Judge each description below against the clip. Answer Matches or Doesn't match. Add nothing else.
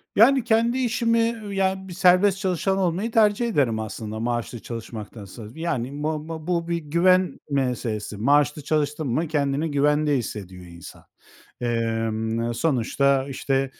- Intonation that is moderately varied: Doesn't match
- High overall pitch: Doesn't match